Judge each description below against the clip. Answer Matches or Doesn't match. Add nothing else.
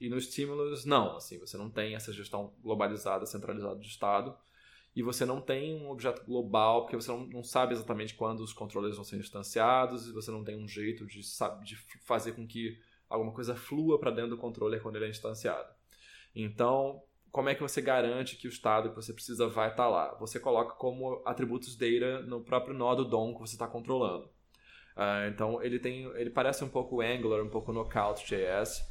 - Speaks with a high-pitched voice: Doesn't match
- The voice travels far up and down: Doesn't match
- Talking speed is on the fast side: Matches